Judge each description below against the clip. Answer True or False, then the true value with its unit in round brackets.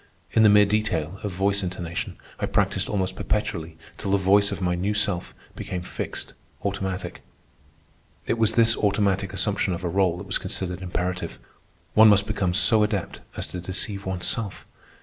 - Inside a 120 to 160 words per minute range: False (170 wpm)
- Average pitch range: False (2.2 semitones)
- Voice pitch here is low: True (95 Hz)